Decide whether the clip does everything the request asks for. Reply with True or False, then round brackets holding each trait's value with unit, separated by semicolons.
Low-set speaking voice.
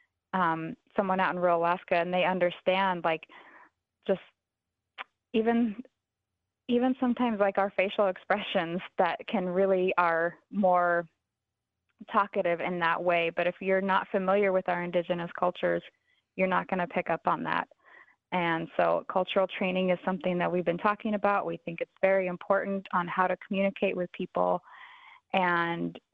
False (185 Hz)